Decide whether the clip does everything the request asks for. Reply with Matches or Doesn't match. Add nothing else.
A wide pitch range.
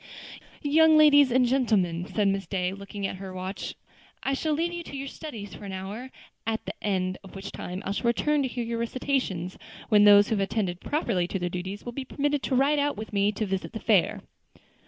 Matches